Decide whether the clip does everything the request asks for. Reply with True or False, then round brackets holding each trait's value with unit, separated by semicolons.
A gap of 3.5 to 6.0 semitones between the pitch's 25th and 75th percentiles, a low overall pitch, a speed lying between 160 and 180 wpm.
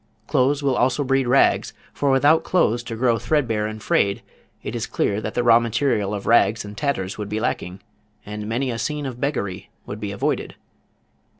False (4.3 semitones; 115 Hz; 190 wpm)